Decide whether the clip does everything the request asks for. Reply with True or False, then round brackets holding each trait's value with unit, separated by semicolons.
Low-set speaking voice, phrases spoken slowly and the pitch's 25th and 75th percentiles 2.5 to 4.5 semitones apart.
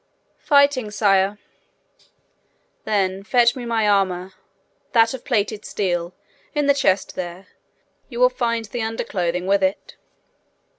False (210 Hz; 120 wpm; 4.0 semitones)